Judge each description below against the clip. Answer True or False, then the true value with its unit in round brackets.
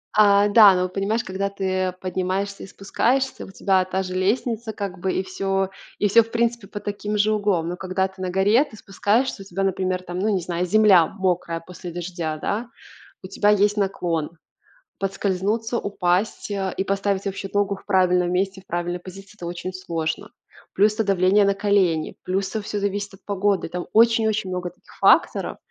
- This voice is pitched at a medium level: False (195 Hz)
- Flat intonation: True (2.0 semitones)